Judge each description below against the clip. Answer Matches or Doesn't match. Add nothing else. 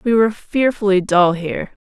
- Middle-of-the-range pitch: Doesn't match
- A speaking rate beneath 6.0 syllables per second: Matches